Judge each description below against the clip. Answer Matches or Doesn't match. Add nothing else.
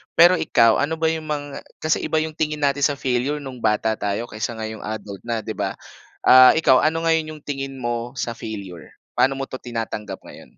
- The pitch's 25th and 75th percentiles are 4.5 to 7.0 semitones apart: Matches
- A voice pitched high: Doesn't match